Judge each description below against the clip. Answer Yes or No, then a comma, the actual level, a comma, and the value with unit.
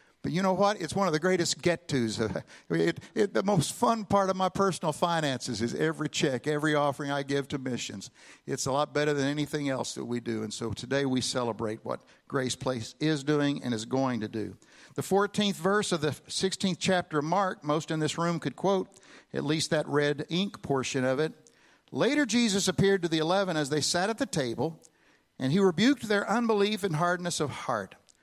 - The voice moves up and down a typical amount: No, wide, 5.8 semitones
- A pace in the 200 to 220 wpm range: Yes, fast, 205 wpm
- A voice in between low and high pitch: Yes, medium, 155 Hz